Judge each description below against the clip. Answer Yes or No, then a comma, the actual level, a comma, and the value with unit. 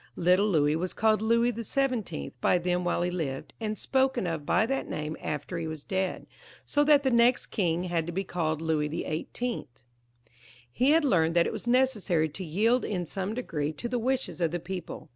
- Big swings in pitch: Yes, wide, 6.3 semitones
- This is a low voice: No, medium, 185 Hz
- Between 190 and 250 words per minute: Yes, average, 200 wpm